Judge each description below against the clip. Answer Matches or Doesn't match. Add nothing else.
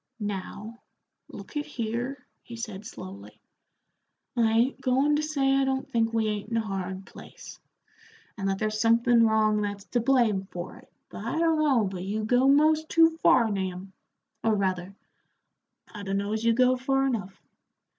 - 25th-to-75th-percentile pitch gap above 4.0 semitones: Matches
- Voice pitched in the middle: Doesn't match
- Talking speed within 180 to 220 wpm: Doesn't match